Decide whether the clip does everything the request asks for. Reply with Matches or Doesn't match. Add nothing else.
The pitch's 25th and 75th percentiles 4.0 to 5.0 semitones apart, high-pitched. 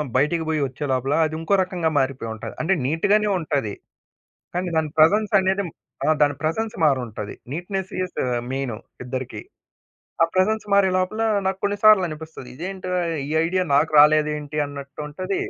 Doesn't match